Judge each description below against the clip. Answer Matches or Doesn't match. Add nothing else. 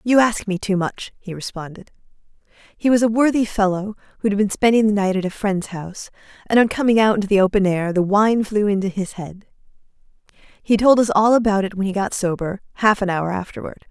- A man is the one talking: Doesn't match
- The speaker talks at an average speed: Doesn't match